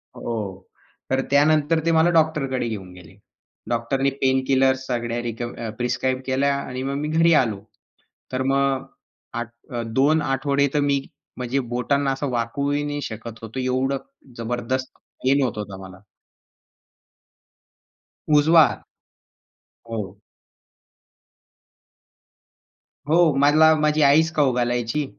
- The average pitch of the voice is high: No, low, 135 Hz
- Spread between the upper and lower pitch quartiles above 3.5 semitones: No, average, 3.2 semitones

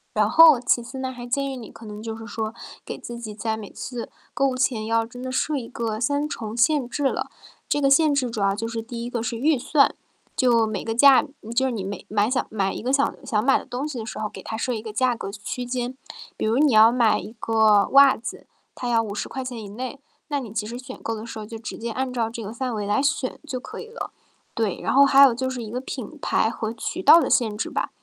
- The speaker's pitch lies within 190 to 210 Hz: No, high, 235 Hz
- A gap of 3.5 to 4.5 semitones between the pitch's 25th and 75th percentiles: No, average, 3.0 semitones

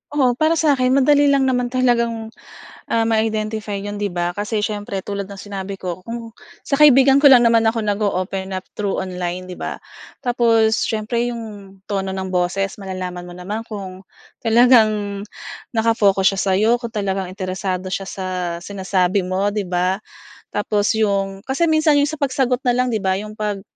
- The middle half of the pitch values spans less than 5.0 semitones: Yes, average, 3.7 semitones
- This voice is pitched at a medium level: No, high, 210 Hz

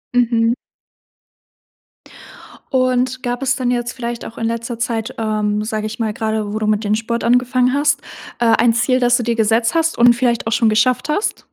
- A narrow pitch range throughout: Yes, narrow, 2.0 semitones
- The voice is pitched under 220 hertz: No, high, 235 Hz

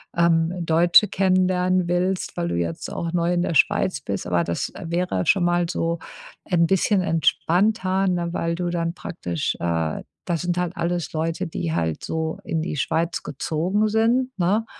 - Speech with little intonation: Yes, narrow, 2.3 semitones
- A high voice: No, medium, 170 Hz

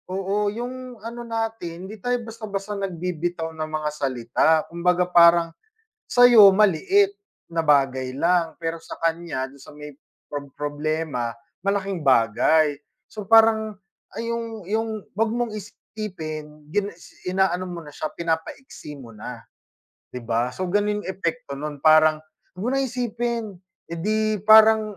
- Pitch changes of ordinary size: No, wide, 5.7 semitones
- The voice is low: No, medium, 180 Hz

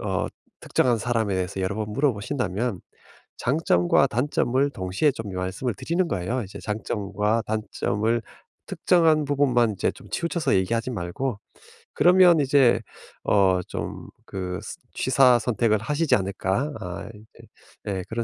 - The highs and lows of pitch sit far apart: Yes, wide, 5.7 semitones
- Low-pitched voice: Yes, low, 115 Hz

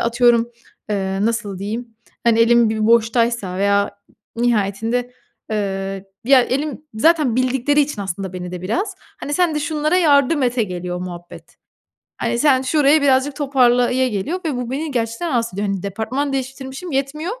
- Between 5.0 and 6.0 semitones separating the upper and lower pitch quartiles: Yes, average, 5.3 semitones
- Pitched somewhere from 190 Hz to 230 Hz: No, high, 240 Hz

